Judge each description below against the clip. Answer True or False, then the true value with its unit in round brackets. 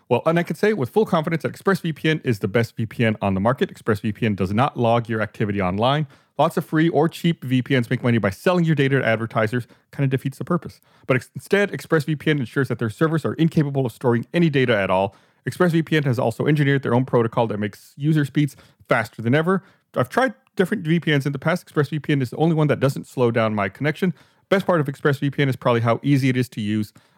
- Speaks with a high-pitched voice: False (140 Hz)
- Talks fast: True (225 wpm)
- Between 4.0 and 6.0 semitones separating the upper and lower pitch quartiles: True (5.2 semitones)